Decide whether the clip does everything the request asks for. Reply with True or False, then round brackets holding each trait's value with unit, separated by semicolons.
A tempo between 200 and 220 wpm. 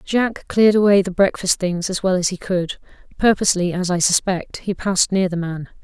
True (205 wpm)